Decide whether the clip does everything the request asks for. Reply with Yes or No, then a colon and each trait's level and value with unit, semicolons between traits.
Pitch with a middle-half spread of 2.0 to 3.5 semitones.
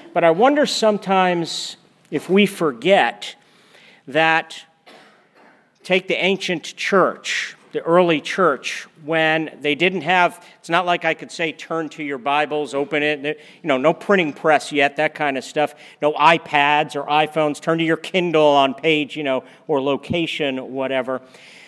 Yes: average, 2.8 semitones